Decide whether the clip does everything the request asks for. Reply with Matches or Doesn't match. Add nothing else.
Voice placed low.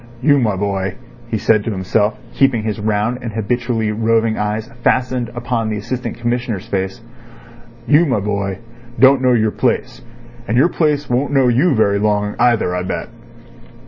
Matches